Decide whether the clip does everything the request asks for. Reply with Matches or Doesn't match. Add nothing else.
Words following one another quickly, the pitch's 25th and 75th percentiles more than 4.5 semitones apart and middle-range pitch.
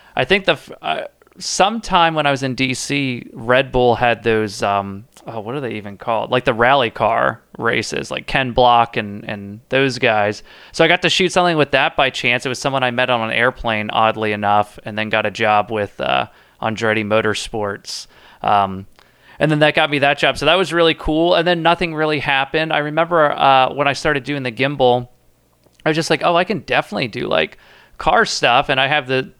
Doesn't match